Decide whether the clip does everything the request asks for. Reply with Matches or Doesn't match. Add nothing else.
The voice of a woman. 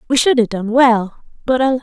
Matches